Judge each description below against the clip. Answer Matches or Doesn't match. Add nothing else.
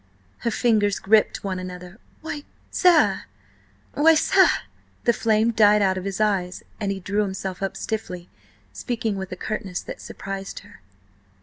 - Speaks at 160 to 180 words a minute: Doesn't match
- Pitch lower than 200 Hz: Doesn't match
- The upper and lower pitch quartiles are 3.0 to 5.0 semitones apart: Doesn't match